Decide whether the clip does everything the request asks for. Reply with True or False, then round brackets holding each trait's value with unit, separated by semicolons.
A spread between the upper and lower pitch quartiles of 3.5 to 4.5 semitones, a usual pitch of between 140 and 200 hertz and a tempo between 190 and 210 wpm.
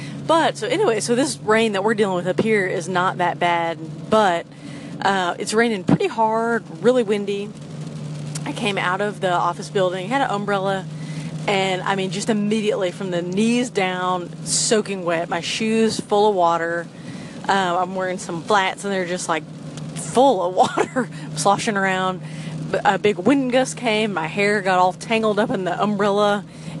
False (3.8 semitones; 190 Hz; 175 wpm)